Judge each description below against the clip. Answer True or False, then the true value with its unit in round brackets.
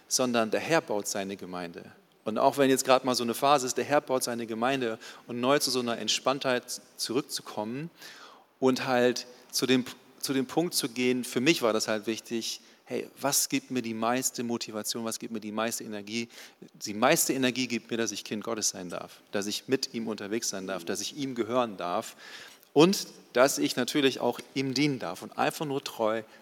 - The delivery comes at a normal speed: False (205 wpm)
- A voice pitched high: False (125 Hz)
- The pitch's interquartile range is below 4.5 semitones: True (2.9 semitones)